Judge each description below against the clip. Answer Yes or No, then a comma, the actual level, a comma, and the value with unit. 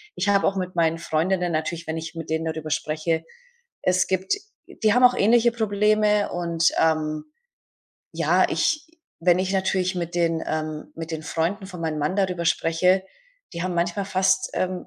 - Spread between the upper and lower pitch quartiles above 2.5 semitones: Yes, average, 2.9 semitones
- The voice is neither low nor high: Yes, medium, 175 Hz